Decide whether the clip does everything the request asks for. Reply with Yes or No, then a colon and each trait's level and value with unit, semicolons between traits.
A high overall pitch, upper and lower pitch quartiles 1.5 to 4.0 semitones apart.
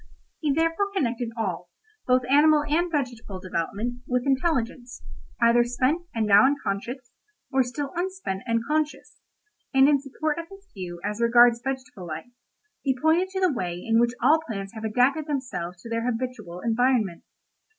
No: very high, 250 Hz; average, 4.7 semitones